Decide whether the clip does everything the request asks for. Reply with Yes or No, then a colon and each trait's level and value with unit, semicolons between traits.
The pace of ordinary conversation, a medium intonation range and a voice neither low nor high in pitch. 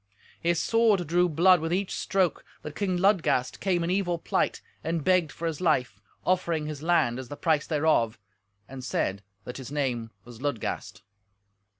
Yes: average, 170 wpm; average, 5.0 semitones; medium, 160 Hz